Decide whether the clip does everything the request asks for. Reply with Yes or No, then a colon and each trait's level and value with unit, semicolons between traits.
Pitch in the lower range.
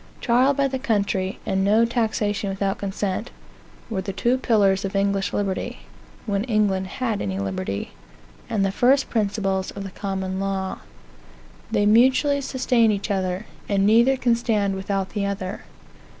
No: high, 200 Hz